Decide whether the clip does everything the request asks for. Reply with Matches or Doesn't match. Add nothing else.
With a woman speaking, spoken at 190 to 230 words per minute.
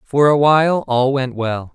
Doesn't match